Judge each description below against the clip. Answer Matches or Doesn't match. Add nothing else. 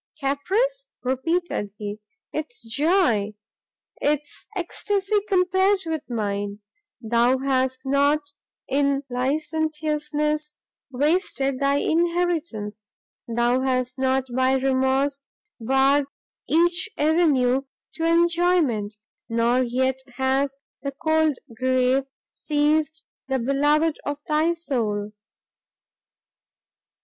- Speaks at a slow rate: Matches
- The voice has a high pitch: Matches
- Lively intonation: Doesn't match